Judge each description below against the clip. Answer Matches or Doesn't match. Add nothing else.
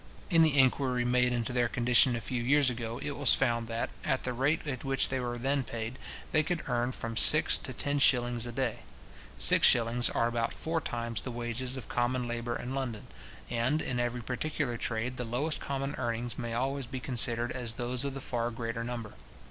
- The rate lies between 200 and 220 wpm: Matches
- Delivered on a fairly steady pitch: Matches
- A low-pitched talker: Matches